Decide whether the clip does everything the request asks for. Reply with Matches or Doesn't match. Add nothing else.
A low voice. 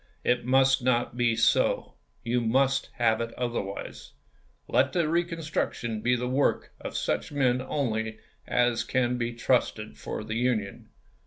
Matches